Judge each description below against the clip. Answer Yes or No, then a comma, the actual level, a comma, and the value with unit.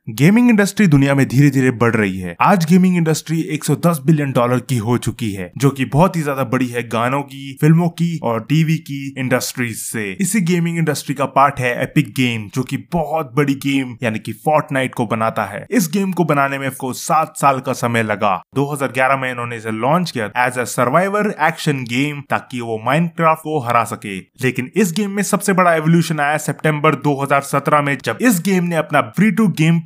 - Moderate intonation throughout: Yes, average, 4.6 semitones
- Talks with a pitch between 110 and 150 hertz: Yes, medium, 140 Hz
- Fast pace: Yes, fast, 200 wpm